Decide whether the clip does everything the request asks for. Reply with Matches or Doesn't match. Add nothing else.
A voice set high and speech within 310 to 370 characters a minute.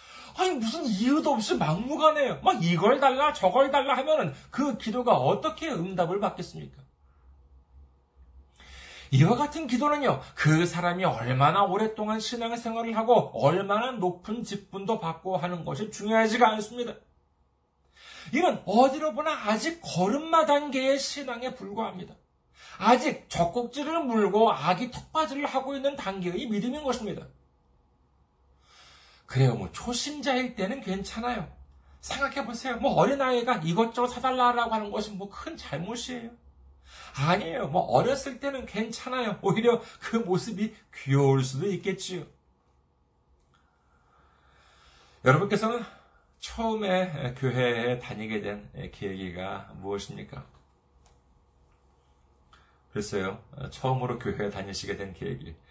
Doesn't match